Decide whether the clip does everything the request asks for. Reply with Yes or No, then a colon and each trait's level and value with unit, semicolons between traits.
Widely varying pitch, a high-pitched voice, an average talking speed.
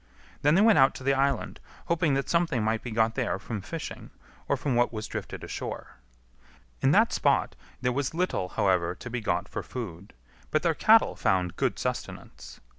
No: wide, 5.9 semitones; low, 125 Hz; average, 190 wpm